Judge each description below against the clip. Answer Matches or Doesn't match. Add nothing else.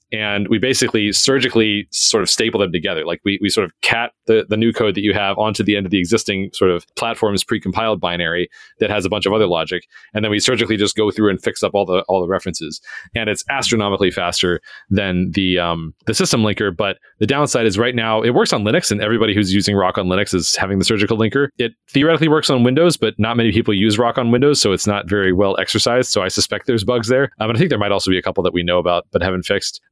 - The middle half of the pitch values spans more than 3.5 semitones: Doesn't match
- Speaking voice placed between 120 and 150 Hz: Doesn't match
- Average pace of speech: Doesn't match